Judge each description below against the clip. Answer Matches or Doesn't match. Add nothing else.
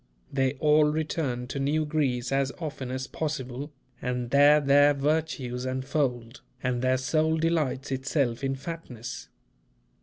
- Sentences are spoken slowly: Matches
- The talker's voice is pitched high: Doesn't match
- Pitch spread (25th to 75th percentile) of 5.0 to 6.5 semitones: Doesn't match